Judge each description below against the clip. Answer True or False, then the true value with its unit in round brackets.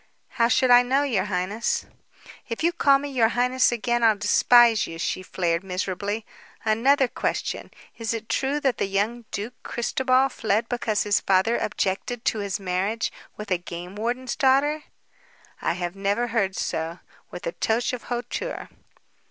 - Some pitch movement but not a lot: True (4.0 semitones)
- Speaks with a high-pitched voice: True (225 Hz)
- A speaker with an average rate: True (160 wpm)